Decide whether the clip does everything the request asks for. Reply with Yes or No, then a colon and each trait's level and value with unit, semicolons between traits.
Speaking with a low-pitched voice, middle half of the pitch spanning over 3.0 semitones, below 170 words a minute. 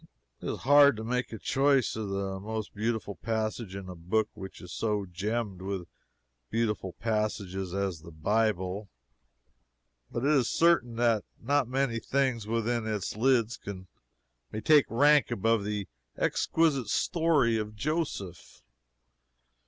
Yes: low, 110 Hz; average, 4.0 semitones; slow, 135 wpm